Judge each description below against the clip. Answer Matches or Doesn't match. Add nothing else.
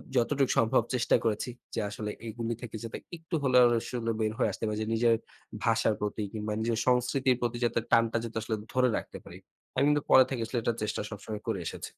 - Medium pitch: Doesn't match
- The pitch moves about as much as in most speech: Doesn't match